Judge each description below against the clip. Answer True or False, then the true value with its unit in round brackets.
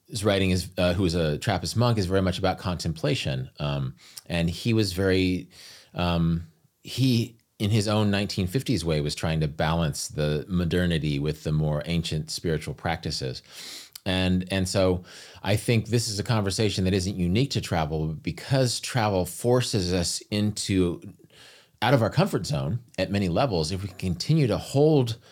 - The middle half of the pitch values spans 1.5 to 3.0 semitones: False (5.0 semitones)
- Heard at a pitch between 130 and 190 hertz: False (95 Hz)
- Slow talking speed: False (170 wpm)